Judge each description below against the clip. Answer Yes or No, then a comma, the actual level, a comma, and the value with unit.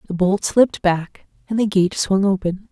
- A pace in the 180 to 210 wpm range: Yes, average, 200 wpm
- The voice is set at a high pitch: Yes, high, 195 Hz